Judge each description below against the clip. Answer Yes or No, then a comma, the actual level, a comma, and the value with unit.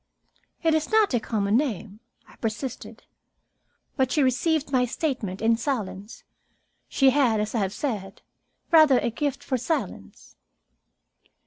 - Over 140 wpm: No, slow, 135 wpm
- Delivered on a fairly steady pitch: No, average, 5.0 semitones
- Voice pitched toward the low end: No, very high, 250 Hz